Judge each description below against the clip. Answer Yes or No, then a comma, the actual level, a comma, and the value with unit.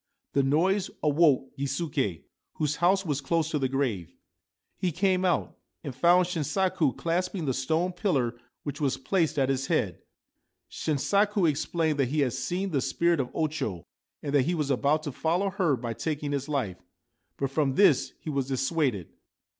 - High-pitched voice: No, medium, 150 Hz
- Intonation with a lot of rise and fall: No, average, 4.3 semitones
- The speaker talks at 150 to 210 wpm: Yes, average, 170 wpm